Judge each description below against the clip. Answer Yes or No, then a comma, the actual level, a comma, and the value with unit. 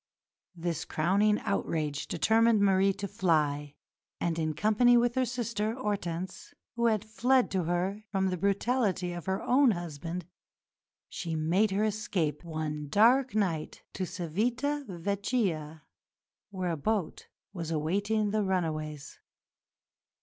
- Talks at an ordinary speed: No, slow, 130 wpm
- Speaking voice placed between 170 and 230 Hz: Yes, high, 190 Hz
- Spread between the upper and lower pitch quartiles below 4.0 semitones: No, average, 4.8 semitones